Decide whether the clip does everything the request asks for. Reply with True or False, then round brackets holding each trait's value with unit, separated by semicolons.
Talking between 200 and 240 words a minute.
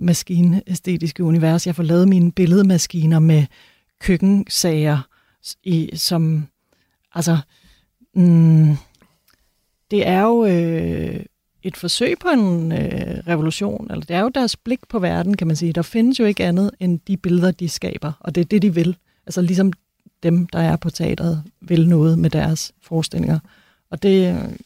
False (155 wpm)